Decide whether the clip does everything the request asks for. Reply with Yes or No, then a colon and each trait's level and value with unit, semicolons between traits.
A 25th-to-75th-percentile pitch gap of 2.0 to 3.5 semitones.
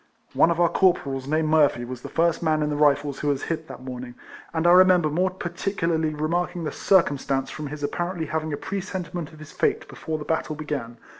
Yes: average, 3.1 semitones